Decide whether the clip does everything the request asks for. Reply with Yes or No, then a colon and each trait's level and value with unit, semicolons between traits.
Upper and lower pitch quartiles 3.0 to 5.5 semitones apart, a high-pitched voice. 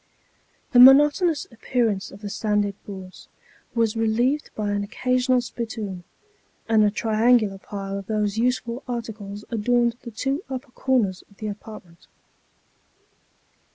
Yes: average, 3.3 semitones; high, 220 Hz